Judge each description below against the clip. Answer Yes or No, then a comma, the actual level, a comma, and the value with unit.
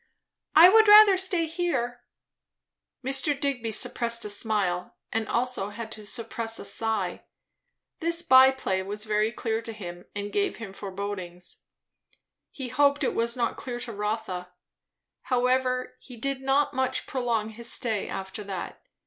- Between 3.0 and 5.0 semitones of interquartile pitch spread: Yes, average, 4.1 semitones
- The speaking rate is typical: Yes, average, 150 wpm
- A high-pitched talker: Yes, high, 235 Hz